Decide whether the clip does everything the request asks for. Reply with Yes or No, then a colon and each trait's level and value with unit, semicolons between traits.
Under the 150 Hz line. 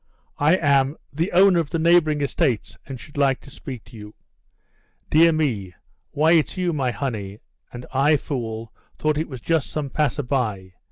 Yes: medium, 140 Hz